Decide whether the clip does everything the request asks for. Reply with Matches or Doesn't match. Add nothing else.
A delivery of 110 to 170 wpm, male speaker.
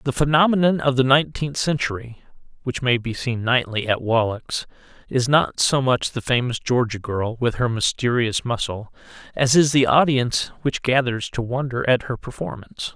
Matches